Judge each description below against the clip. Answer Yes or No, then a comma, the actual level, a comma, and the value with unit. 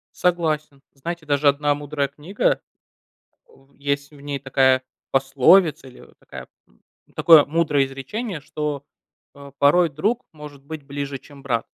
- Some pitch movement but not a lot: No, narrow, 2.1 semitones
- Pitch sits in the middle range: Yes, medium, 145 Hz